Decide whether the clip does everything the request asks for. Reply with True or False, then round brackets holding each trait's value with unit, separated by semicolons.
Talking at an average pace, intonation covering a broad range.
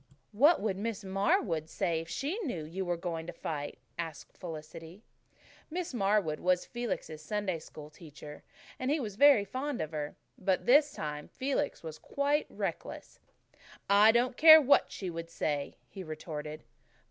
True (160 wpm; 7.5 semitones)